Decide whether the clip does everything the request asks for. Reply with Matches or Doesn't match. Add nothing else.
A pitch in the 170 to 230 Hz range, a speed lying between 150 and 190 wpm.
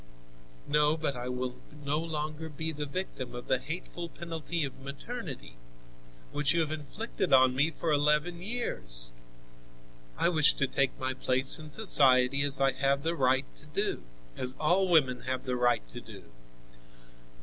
Doesn't match